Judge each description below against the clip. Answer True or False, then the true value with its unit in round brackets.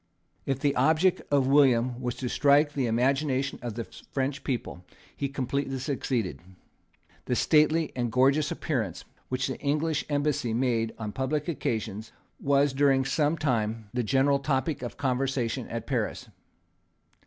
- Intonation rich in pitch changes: False (2.8 semitones)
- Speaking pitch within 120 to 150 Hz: True (135 Hz)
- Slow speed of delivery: False (145 wpm)